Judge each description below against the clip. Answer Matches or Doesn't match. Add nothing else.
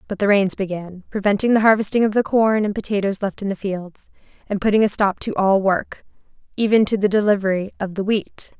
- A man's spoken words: Doesn't match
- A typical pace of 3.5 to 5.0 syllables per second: Doesn't match